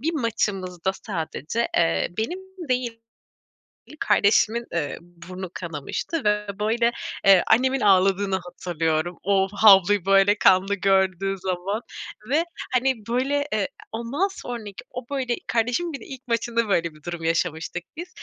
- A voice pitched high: Yes, high, 200 Hz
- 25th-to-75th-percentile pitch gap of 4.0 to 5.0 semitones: Yes, average, 4.6 semitones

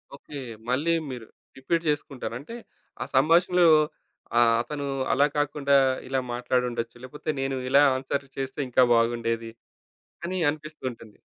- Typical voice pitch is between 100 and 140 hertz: Yes, low, 135 Hz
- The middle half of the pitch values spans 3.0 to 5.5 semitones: Yes, average, 3.4 semitones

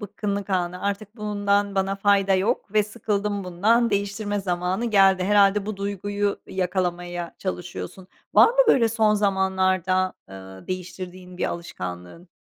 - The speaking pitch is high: Yes, high, 195 Hz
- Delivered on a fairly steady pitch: Yes, narrow, 2.0 semitones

